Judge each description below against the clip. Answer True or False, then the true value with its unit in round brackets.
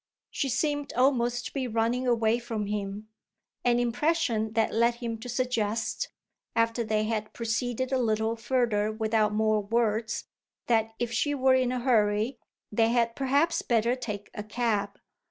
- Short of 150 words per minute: False (155 wpm)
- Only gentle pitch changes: True (2.2 semitones)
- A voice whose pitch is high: True (230 Hz)